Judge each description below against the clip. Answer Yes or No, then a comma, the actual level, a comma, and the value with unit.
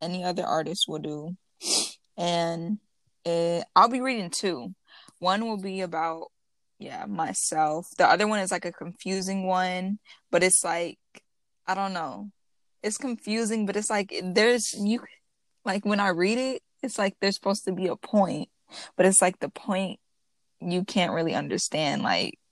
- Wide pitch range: No, average, 3.1 semitones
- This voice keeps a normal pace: Yes, average, 165 wpm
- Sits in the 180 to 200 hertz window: Yes, high, 190 Hz